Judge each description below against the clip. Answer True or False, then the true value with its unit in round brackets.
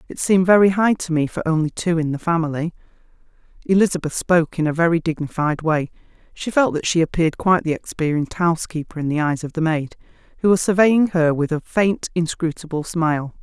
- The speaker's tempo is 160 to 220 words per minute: True (190 wpm)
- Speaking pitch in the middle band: True (165 Hz)